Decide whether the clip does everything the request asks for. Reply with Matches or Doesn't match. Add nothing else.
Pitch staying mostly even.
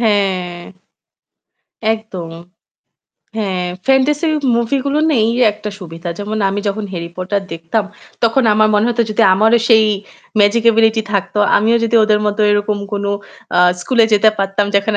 Matches